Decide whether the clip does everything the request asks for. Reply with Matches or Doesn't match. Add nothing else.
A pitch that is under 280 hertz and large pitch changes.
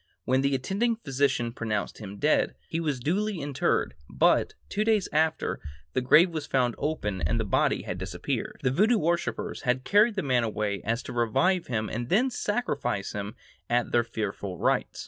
Matches